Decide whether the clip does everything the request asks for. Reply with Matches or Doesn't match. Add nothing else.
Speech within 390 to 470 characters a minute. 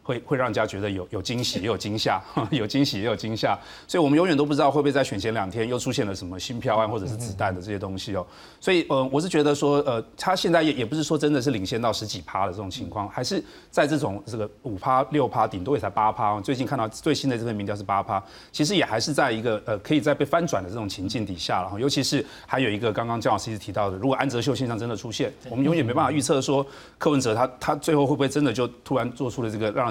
Matches